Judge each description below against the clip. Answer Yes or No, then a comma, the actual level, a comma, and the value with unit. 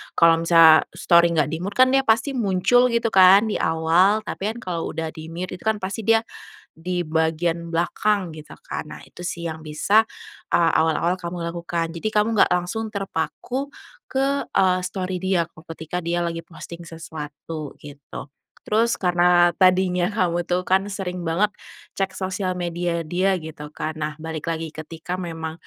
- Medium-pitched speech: Yes, medium, 175 Hz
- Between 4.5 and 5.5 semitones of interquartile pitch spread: No, average, 2.9 semitones